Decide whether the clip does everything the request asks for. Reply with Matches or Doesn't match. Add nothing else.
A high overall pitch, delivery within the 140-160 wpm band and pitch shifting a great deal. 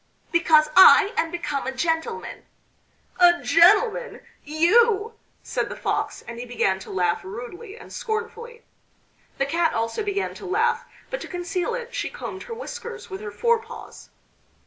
Matches